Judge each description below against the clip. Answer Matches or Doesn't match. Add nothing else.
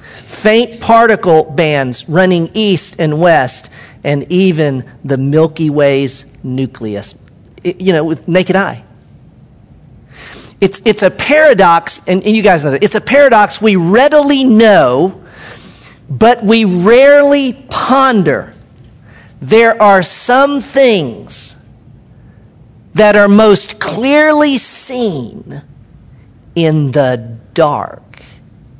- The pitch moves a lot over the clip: Matches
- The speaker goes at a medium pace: Doesn't match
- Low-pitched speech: Doesn't match